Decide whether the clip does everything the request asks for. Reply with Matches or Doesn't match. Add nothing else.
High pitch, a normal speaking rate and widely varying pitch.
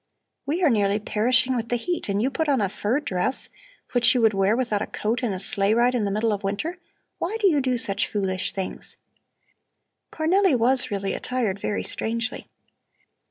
Doesn't match